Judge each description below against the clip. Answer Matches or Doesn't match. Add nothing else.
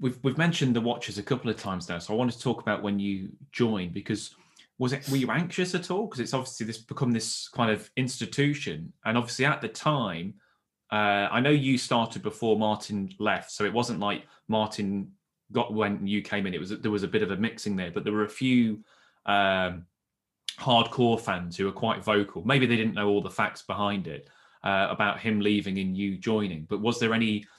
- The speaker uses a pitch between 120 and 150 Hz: Doesn't match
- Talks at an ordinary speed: Doesn't match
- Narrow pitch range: Doesn't match